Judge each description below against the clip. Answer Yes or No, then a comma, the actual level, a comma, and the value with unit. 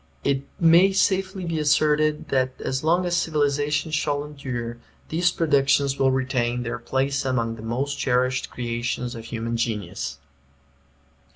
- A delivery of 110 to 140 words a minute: Yes, slow, 135 wpm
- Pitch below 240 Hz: Yes, low, 135 Hz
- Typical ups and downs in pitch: Yes, average, 4.1 semitones